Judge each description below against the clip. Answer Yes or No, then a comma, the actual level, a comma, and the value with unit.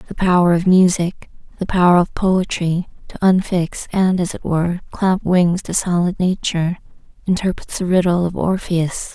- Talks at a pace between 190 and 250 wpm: No, average, 155 wpm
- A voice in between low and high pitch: Yes, medium, 180 Hz